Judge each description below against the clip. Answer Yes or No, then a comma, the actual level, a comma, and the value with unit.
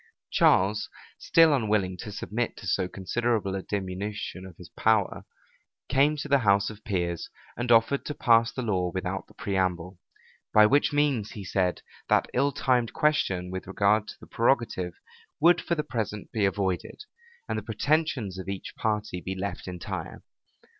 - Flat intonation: No, average, 4.4 semitones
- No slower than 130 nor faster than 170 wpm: Yes, average, 160 wpm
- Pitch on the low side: Yes, low, 105 Hz